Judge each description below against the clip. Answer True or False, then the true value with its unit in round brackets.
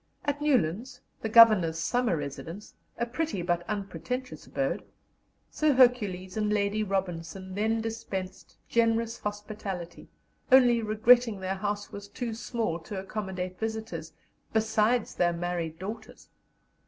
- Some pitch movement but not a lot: True (3.8 semitones)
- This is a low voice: False (210 Hz)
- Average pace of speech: False (120 wpm)